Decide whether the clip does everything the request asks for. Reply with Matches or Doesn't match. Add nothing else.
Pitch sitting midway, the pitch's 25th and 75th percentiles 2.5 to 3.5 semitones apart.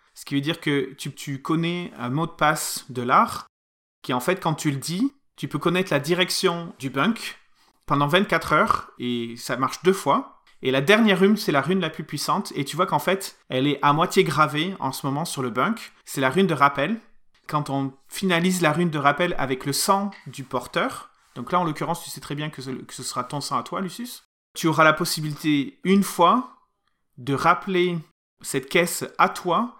Doesn't match